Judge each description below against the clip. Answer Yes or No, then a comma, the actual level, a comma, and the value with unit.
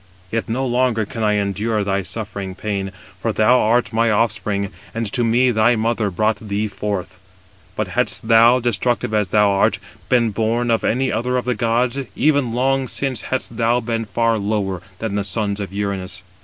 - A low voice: Yes, low, 110 Hz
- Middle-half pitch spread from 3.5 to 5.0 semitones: No, average, 2.8 semitones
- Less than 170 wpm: No, average, 185 wpm